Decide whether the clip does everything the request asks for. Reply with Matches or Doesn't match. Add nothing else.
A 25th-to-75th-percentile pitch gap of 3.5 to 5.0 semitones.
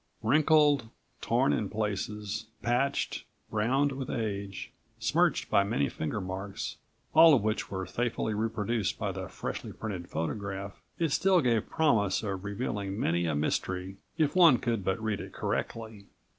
Matches